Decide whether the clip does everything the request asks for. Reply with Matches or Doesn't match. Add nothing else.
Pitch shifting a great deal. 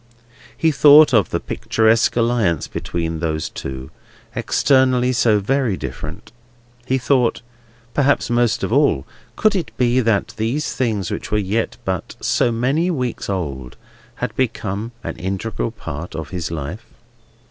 Matches